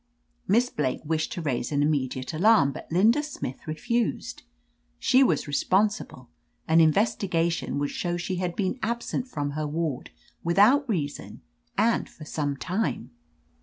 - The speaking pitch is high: No, medium, 170 Hz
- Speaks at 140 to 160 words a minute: Yes, average, 145 wpm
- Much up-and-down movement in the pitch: Yes, wide, 6.9 semitones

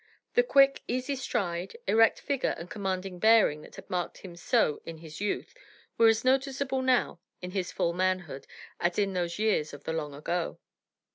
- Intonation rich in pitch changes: Yes, wide, 5.9 semitones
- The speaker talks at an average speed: Yes, average, 180 wpm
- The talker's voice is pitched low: No, high, 190 Hz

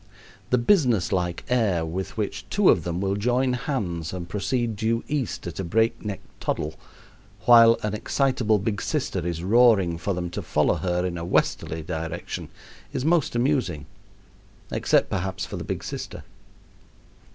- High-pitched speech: No, low, 100 Hz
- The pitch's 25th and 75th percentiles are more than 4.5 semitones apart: Yes, wide, 5.6 semitones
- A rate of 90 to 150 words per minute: No, average, 160 wpm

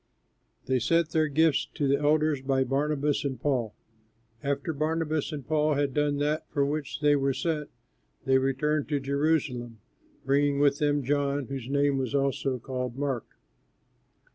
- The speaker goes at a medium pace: Yes, average, 150 wpm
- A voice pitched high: No, medium, 140 Hz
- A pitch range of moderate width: No, narrow, 1.9 semitones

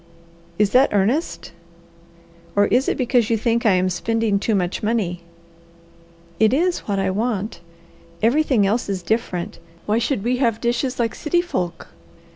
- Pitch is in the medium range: No, high, 225 Hz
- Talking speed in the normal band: Yes, average, 155 wpm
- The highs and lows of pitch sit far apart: No, average, 3.8 semitones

